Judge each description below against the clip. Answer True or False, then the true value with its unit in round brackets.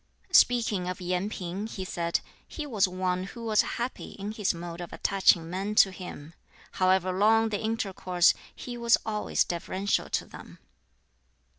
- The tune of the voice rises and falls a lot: False (3.2 semitones)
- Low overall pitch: False (190 Hz)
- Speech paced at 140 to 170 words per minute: True (155 wpm)